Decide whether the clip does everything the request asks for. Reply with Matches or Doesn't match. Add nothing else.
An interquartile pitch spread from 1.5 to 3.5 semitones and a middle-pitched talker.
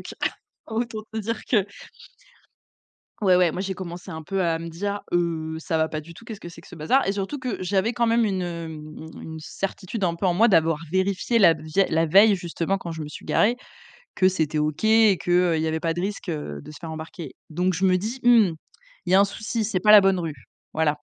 Doesn't match